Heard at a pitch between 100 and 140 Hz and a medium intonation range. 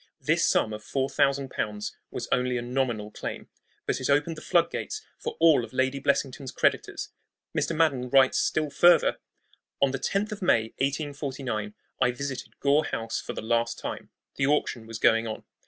Yes: low, 135 Hz; average, 3.5 semitones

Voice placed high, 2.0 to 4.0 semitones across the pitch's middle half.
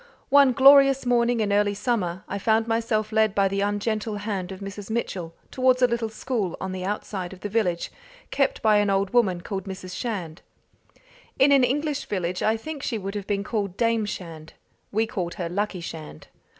Yes: high, 205 Hz; average, 3.5 semitones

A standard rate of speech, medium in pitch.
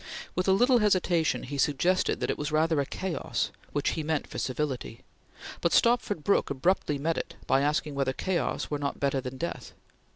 Yes: average, 190 wpm; medium, 155 Hz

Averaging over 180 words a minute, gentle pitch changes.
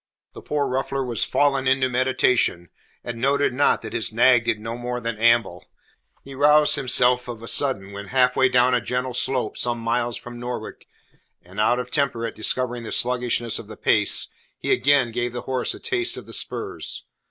Yes: average, 200 wpm; narrow, 2.0 semitones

